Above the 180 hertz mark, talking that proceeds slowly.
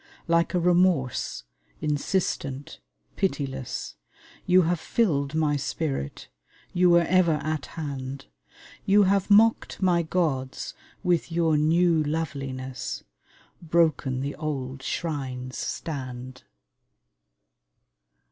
No: medium, 155 Hz; slow, 95 wpm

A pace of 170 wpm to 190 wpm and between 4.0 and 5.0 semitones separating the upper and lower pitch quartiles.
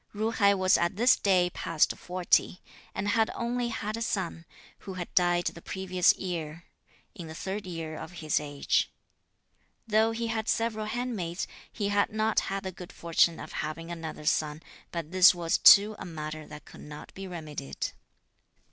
Yes: average, 175 wpm; average, 4.3 semitones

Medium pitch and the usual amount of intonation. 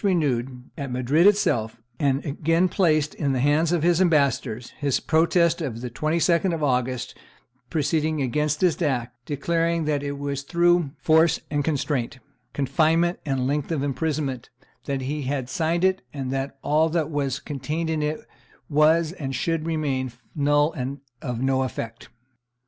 Yes: medium, 145 Hz; average, 3.3 semitones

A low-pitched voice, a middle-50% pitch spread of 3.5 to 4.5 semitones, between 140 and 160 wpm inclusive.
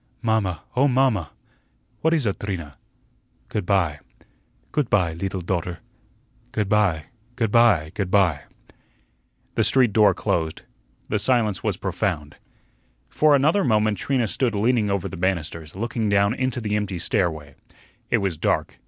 No: low, 100 Hz; average, 4.9 semitones; average, 145 wpm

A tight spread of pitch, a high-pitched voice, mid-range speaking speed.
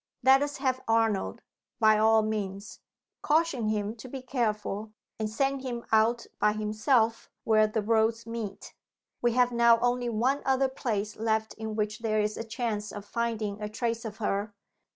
Yes: narrow, 2.2 semitones; high, 225 Hz; average, 170 wpm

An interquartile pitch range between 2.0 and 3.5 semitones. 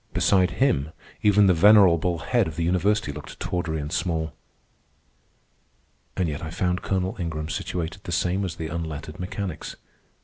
Yes: average, 2.9 semitones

